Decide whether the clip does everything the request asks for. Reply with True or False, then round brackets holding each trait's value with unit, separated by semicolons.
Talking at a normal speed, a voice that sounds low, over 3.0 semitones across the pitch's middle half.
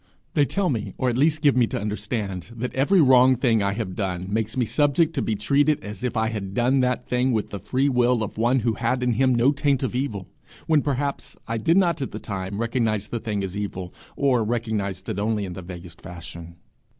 False (230 wpm; 115 Hz; 4.5 semitones)